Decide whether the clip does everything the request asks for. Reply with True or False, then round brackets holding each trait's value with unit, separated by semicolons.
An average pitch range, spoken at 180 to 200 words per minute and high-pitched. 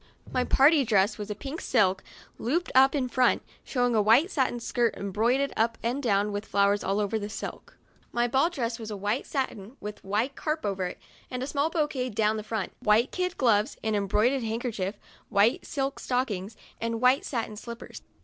True (4.1 semitones; 190 wpm; 230 Hz)